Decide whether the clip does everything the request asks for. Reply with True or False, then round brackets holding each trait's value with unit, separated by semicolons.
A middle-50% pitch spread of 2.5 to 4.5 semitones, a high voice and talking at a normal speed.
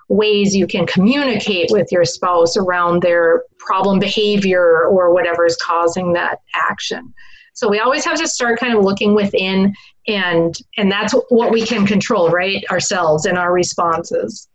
True (3.6 semitones; 195 Hz; 160 wpm)